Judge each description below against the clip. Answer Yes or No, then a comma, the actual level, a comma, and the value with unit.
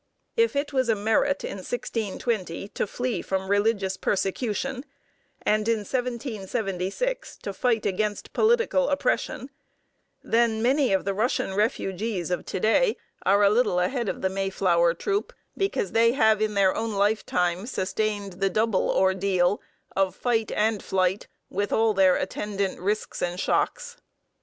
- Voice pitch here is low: No, high, 210 Hz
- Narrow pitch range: No, average, 4.0 semitones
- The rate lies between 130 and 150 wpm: Yes, average, 145 wpm